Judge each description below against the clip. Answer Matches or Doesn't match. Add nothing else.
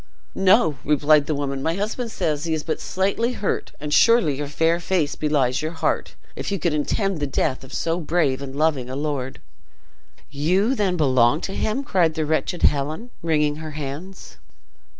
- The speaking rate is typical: Matches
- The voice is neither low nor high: Matches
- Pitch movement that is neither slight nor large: Matches